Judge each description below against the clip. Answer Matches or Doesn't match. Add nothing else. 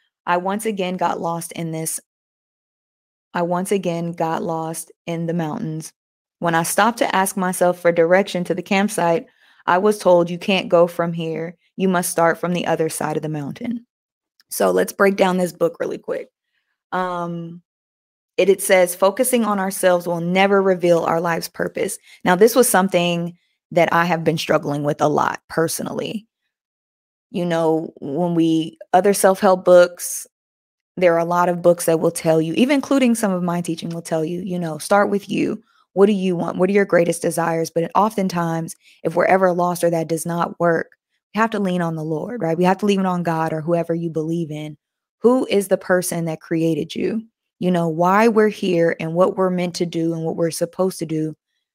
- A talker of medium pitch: Matches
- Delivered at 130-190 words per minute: Doesn't match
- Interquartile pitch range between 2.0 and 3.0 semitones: Matches